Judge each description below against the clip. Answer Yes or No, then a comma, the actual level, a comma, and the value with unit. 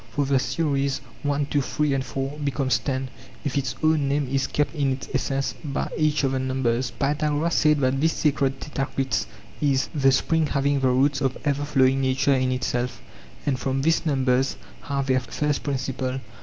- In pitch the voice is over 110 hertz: Yes, low, 135 Hz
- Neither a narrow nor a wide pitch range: No, narrow, 1.7 semitones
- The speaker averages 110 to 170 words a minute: No, average, 185 wpm